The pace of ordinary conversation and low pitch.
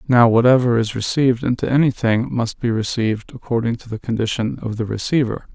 Yes: average, 175 wpm; low, 120 Hz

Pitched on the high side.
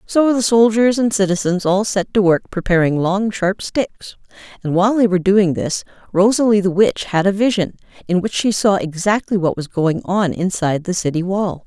Yes: high, 195 Hz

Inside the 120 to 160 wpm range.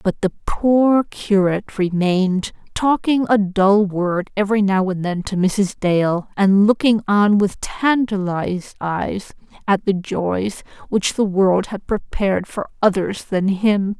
Yes: average, 145 wpm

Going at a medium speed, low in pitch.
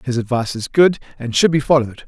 No: fast, 230 wpm; low, 130 Hz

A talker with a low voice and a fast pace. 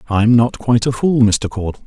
Yes: low, 115 Hz; fast, 225 wpm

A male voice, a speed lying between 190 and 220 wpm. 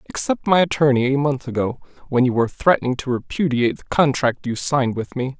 Yes: male; average, 200 wpm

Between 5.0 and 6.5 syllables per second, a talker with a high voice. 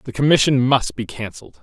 No: 5.7 syllables/s; low, 120 Hz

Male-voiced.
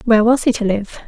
No: female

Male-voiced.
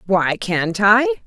No: female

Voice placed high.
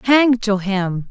Yes: high, 215 Hz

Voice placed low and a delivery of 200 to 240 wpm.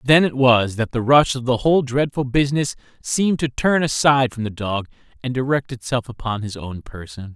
Yes: low, 125 Hz; fast, 205 wpm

